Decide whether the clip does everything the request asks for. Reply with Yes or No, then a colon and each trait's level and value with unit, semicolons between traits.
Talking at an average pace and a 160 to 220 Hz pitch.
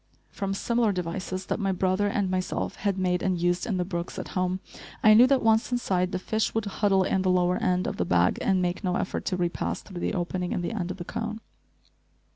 No: fast, 235 wpm; medium, 185 Hz